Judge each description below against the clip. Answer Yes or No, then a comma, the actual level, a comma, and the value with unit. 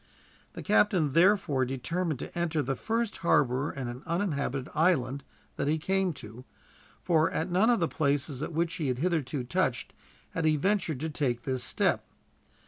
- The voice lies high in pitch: No, medium, 155 Hz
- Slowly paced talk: No, average, 170 wpm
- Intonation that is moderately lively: Yes, average, 4.6 semitones